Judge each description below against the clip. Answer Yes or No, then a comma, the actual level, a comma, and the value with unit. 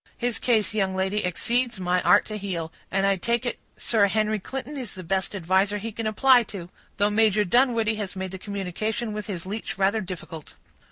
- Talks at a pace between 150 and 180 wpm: No, average, 200 wpm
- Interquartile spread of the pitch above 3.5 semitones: No, average, 2.8 semitones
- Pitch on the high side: Yes, high, 205 Hz